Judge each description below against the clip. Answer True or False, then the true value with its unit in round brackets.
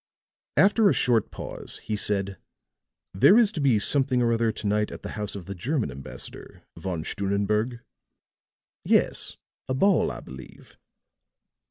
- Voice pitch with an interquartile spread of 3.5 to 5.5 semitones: True (4.9 semitones)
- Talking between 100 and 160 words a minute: True (150 wpm)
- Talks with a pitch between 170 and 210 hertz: False (110 Hz)